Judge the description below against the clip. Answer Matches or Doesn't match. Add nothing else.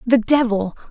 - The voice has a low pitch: Doesn't match